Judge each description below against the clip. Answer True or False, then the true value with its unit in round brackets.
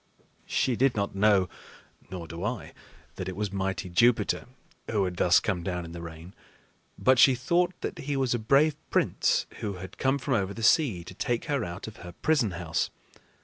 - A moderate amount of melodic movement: False (6.1 semitones)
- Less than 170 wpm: False (195 wpm)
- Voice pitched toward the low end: True (105 Hz)